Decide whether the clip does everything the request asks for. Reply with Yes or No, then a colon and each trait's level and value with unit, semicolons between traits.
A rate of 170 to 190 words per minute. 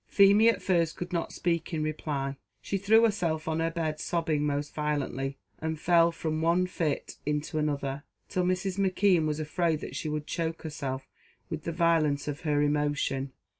Yes: average, 175 wpm